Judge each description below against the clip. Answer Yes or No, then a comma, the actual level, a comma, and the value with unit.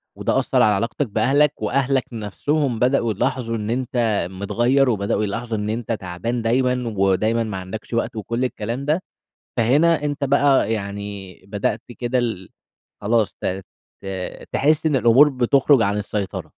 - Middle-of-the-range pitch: No, low, 115 Hz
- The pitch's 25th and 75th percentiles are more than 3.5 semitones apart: Yes, average, 4.0 semitones